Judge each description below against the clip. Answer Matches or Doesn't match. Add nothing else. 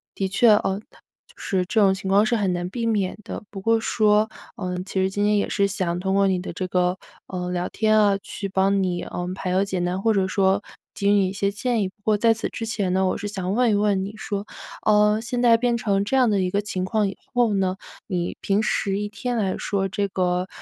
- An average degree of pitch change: Doesn't match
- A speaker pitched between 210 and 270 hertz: Doesn't match